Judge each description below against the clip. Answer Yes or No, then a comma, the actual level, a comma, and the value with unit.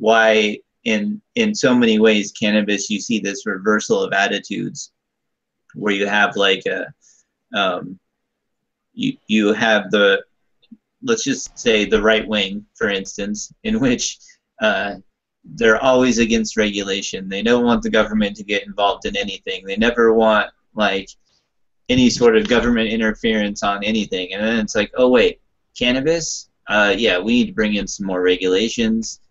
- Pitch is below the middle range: Yes, low, 110 Hz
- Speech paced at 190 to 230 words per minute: No, average, 155 wpm